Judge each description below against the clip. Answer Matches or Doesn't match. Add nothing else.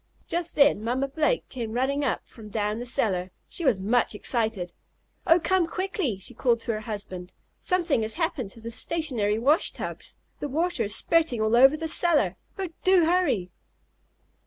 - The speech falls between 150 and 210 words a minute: Matches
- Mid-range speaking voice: Doesn't match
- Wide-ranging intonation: Matches